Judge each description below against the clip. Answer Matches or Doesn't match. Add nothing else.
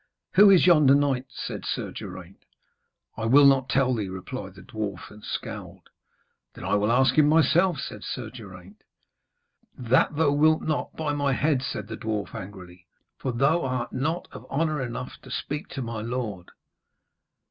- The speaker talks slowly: Doesn't match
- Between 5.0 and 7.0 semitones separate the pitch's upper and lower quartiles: Matches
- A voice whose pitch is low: Matches